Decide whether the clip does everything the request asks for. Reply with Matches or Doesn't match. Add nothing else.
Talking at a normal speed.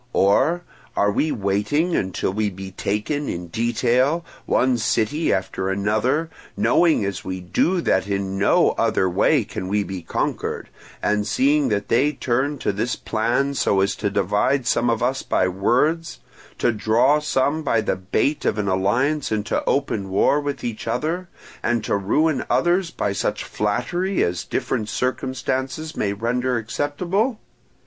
Matches